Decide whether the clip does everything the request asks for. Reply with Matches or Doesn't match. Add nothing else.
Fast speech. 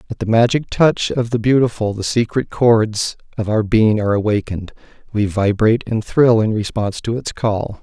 Doesn't match